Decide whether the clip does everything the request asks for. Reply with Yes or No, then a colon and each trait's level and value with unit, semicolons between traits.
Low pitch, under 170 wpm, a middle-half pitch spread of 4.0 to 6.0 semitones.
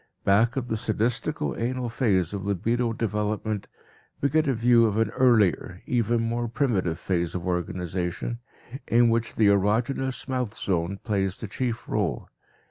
No: low, 110 Hz; average, 150 wpm; average, 3.6 semitones